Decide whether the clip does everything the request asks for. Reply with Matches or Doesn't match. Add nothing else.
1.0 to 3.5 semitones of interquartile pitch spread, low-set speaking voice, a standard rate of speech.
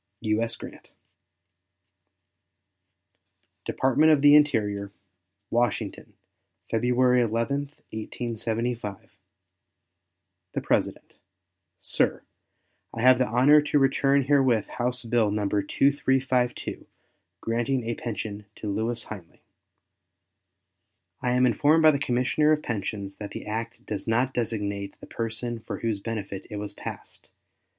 Doesn't match